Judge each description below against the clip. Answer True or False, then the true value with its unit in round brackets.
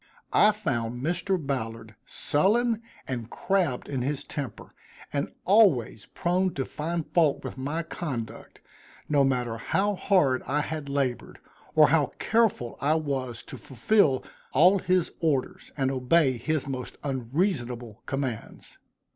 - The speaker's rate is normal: False (130 wpm)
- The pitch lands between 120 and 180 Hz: True (140 Hz)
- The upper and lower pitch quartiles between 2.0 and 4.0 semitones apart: False (5.5 semitones)